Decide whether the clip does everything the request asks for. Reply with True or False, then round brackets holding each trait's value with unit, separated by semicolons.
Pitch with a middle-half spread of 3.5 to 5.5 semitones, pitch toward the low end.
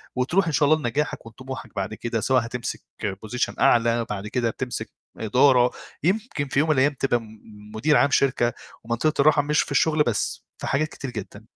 True (4.1 semitones; 125 Hz)